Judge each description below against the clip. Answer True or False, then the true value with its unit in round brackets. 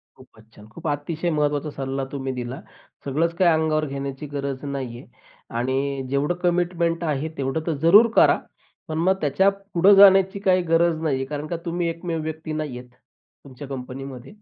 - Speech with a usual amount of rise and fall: True (3.7 semitones)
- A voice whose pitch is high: False (150 Hz)